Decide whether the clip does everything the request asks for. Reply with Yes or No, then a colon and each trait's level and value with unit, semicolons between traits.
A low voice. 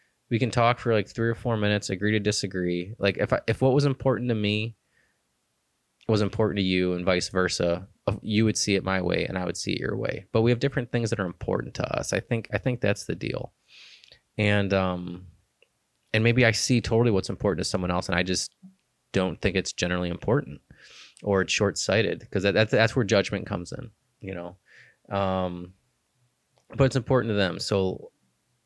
Yes: low, 105 Hz